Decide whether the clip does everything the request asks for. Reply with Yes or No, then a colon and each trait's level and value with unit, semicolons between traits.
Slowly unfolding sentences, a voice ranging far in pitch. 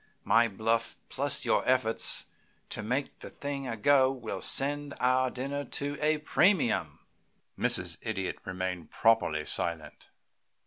Yes: slow, 130 wpm; wide, 6.1 semitones